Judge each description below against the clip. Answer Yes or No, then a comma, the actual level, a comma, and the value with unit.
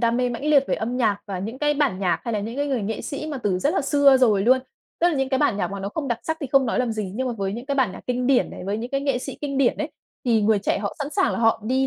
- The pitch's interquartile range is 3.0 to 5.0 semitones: Yes, average, 4.3 semitones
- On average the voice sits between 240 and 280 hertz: Yes, very high, 250 Hz